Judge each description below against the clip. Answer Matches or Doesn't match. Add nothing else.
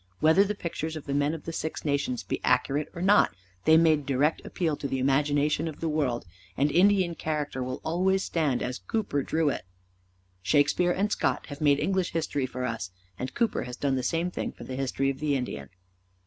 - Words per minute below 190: Doesn't match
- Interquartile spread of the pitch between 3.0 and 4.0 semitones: Matches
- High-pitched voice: Doesn't match